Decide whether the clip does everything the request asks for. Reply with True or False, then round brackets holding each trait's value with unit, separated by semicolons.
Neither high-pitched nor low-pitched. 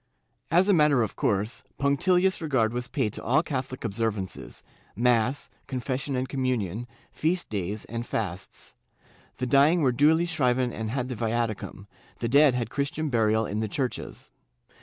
False (125 Hz)